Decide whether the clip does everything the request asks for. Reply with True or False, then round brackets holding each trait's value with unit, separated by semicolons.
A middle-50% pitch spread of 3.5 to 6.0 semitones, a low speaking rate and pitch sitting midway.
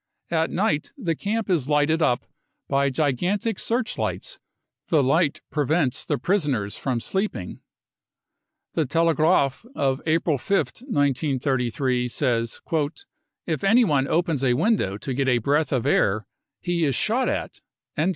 True (5.1 semitones; 130 wpm; 150 Hz)